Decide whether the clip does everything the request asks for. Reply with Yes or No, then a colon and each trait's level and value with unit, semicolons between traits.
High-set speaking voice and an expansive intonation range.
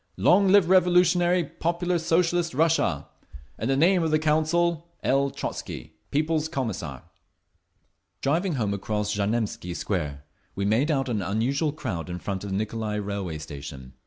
No: low, 135 Hz; wide, 8.8 semitones